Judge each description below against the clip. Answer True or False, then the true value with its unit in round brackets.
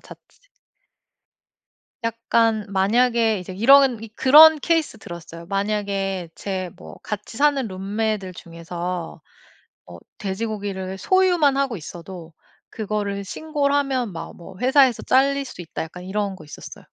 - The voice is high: True (210 Hz)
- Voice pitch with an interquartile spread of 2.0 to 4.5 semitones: False (5.6 semitones)